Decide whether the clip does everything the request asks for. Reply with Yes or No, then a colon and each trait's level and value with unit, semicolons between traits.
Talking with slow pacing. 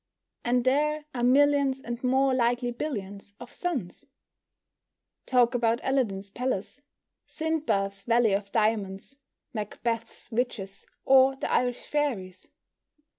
Yes: slow, 110 wpm